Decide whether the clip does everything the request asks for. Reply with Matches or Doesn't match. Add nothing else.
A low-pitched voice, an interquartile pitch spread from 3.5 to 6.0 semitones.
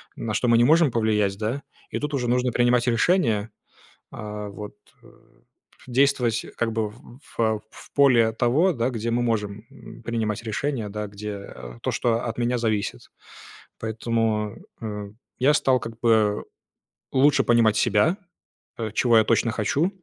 Doesn't match